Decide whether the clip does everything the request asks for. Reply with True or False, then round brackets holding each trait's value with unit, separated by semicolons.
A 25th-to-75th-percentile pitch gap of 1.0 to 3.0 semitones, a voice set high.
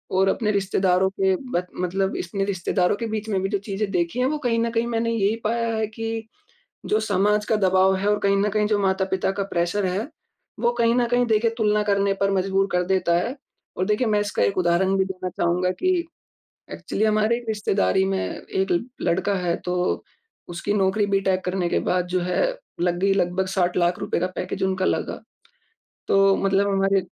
True (2.4 semitones; 195 Hz)